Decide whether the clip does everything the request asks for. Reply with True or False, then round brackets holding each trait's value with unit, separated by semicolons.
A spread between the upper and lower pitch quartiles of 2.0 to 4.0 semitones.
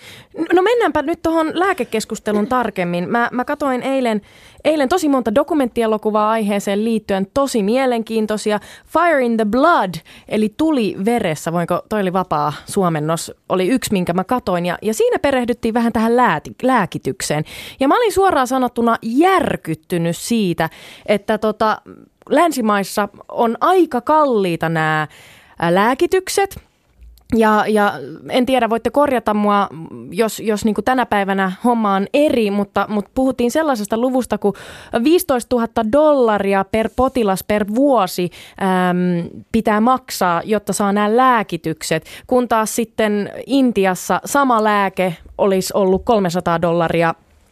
False (5.1 semitones)